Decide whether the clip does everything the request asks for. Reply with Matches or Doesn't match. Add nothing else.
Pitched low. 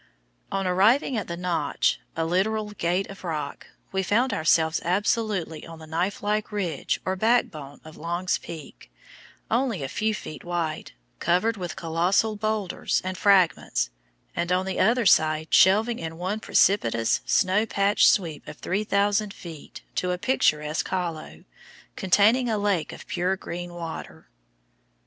Doesn't match